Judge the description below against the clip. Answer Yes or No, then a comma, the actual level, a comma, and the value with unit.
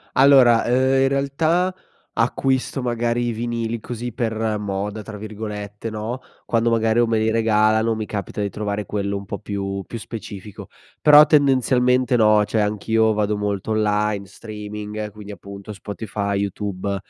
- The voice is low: Yes, low, 110 Hz